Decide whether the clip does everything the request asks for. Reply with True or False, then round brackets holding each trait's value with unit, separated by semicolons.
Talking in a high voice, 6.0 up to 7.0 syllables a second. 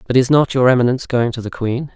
False (125 Hz; 6.7 syllables/s)